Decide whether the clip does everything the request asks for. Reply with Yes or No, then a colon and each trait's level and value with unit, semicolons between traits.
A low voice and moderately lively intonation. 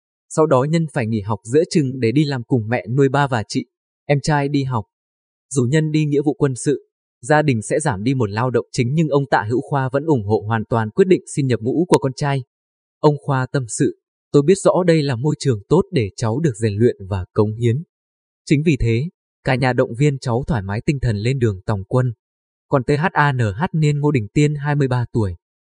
Yes: low, 130 Hz; average, 4.6 semitones